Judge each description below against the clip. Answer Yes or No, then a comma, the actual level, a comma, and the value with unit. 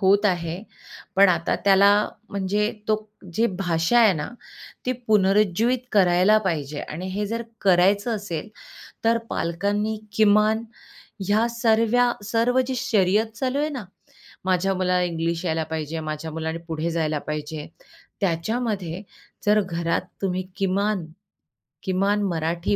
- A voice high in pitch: Yes, high, 195 Hz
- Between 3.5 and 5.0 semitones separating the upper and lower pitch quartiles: Yes, average, 4.2 semitones